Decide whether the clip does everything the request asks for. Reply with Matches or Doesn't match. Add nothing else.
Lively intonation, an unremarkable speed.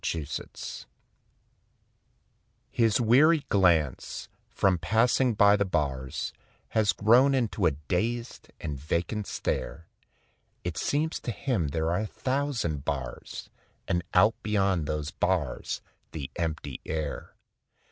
Doesn't match